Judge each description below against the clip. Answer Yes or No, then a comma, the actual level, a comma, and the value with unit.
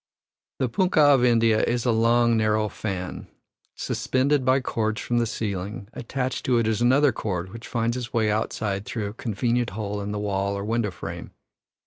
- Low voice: Yes, low, 115 Hz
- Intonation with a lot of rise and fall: No, average, 2.8 semitones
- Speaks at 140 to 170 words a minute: No, average, 180 wpm